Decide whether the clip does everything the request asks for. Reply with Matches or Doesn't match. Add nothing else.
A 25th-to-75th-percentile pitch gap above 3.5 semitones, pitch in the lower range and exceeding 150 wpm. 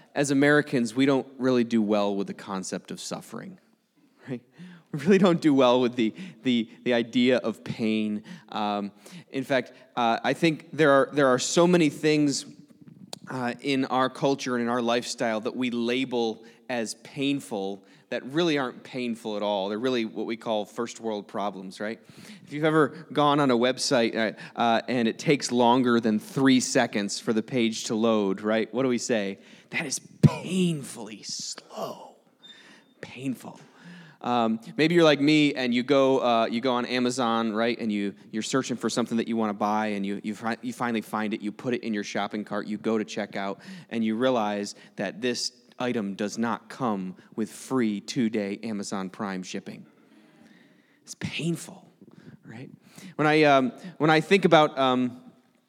Matches